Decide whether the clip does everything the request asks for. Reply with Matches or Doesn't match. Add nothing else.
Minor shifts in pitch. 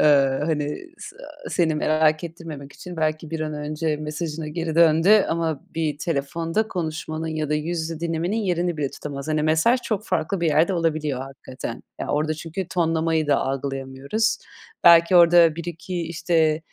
Matches